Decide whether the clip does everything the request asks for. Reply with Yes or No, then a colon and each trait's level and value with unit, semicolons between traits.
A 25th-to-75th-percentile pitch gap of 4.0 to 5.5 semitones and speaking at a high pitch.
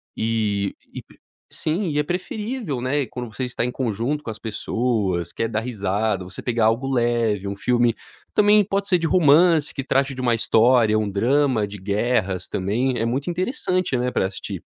No: average, 5.2 semitones; low, 120 Hz